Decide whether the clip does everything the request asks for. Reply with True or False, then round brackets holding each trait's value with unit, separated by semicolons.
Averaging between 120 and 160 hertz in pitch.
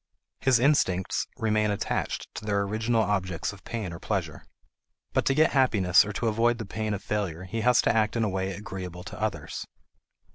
False (105 Hz)